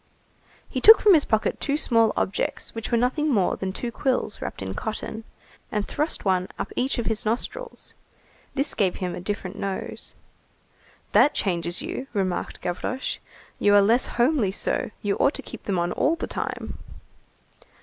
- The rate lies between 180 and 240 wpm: No, average, 170 wpm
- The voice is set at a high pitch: Yes, high, 220 Hz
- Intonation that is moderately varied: No, wide, 5.7 semitones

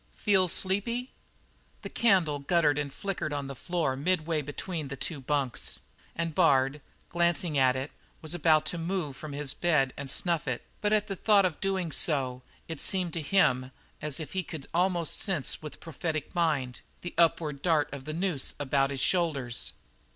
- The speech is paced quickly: No, average, 175 wpm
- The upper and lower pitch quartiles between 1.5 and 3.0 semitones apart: No, average, 4.1 semitones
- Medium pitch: Yes, medium, 155 Hz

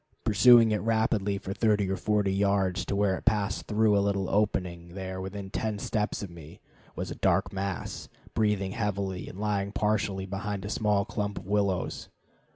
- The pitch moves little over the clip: Yes, narrow, 1.6 semitones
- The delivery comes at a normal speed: Yes, average, 175 wpm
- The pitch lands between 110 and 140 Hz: No, low, 100 Hz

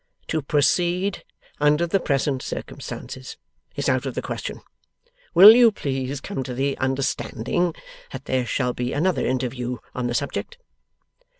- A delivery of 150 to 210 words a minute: No, average, 140 wpm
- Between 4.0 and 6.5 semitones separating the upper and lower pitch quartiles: Yes, average, 5.0 semitones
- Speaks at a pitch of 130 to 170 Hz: Yes, medium, 140 Hz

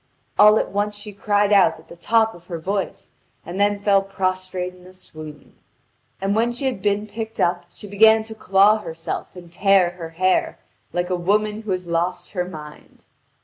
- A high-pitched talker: Yes, high, 195 Hz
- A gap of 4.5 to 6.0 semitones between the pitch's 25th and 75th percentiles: No, average, 2.9 semitones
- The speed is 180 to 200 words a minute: Yes, average, 190 wpm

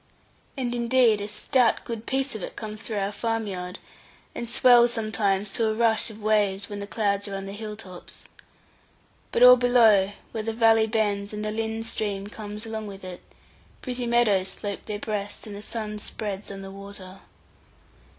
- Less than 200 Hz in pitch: No, high, 215 Hz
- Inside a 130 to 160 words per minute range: No, average, 185 wpm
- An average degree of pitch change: No, narrow, 2.1 semitones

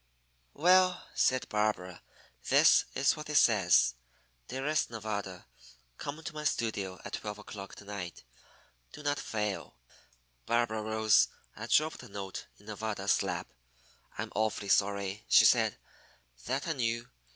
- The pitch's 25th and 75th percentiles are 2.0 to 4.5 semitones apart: No, average, 5.0 semitones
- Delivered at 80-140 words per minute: Yes, slow, 135 wpm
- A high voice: No, low, 110 Hz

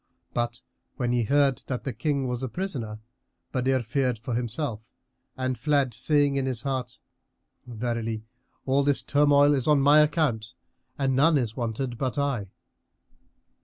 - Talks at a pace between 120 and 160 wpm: Yes, average, 150 wpm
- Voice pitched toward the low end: Yes, low, 130 Hz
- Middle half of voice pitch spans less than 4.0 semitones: Yes, average, 3.0 semitones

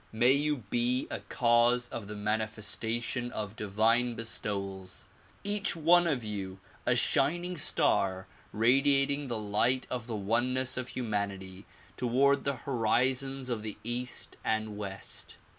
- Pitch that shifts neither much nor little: Yes, average, 3.7 semitones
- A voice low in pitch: Yes, low, 120 Hz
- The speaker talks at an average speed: No, slow, 130 wpm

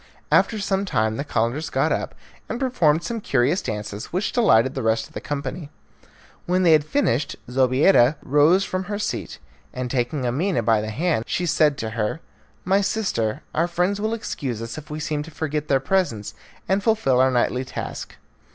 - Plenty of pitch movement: Yes, wide, 7.2 semitones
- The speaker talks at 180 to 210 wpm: Yes, average, 185 wpm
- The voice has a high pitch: No, medium, 150 Hz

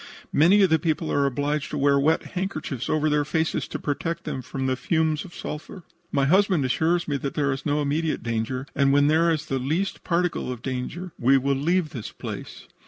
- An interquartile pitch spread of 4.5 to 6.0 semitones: No, average, 3.2 semitones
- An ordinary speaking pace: No, fast, 210 wpm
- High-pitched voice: No, medium, 150 Hz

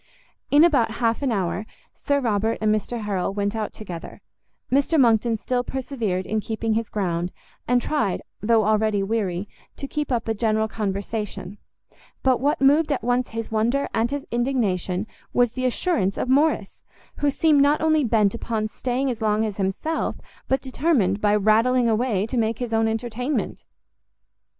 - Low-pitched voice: No, high, 225 Hz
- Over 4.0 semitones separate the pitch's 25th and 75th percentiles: No, average, 3.6 semitones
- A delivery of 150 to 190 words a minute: Yes, average, 165 wpm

